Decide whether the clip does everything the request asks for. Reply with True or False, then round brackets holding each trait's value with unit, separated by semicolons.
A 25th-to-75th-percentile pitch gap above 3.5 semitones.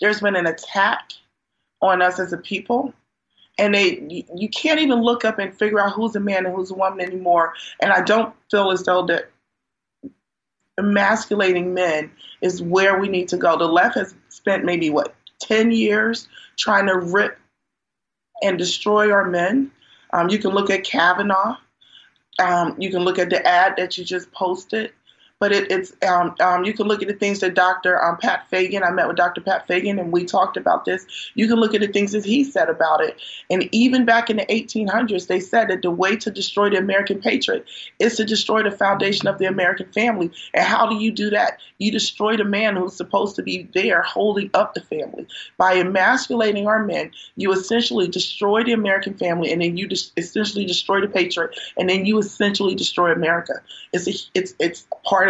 False (3.1 semitones)